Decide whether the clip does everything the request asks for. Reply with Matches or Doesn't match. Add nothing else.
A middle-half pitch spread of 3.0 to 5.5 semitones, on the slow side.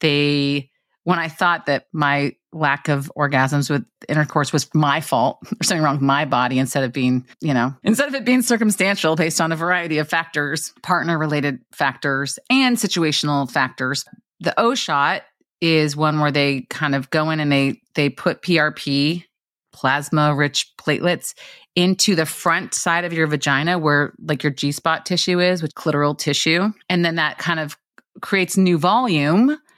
Doesn't match